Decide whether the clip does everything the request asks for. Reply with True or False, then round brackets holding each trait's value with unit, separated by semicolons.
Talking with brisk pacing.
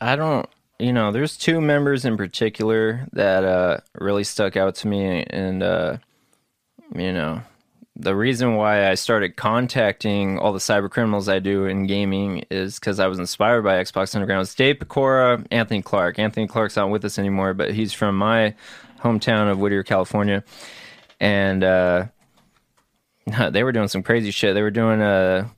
False (175 wpm)